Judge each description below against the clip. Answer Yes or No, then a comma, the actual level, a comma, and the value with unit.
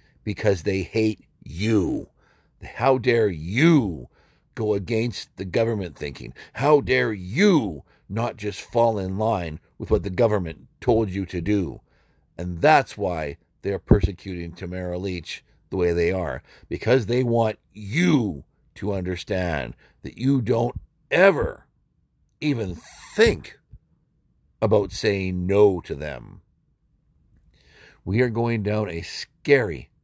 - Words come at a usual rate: No, slow, 125 wpm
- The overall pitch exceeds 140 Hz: No, low, 100 Hz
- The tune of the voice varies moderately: Yes, average, 4.5 semitones